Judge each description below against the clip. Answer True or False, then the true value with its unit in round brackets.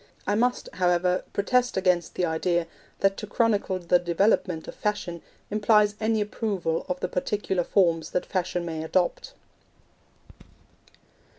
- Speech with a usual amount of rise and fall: True (3.2 semitones)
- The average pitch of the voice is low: False (185 Hz)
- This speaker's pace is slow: True (130 wpm)